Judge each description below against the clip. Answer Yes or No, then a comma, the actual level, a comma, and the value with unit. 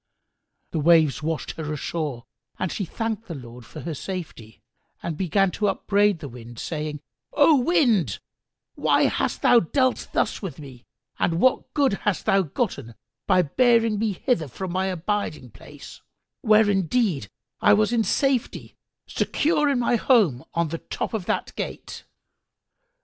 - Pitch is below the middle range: No, medium, 185 Hz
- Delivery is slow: No, average, 150 wpm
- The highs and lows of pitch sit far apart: Yes, wide, 6.7 semitones